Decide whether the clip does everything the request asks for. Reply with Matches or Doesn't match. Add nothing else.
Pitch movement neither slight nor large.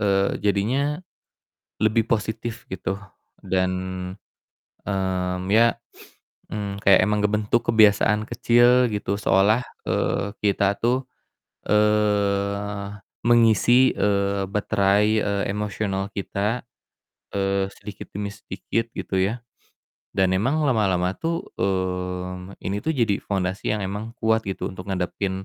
Doesn't match